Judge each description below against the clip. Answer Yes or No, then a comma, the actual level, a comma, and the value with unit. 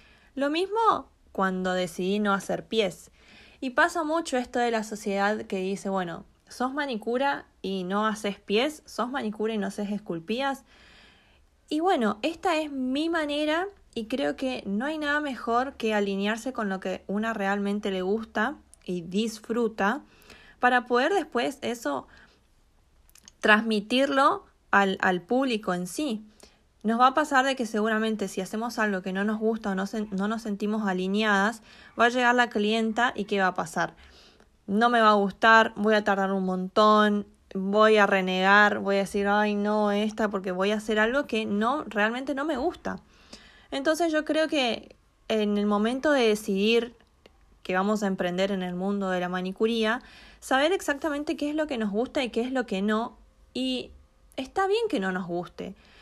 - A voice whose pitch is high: Yes, high, 220 Hz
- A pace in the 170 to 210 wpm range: Yes, average, 175 wpm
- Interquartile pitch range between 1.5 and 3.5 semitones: No, average, 4.2 semitones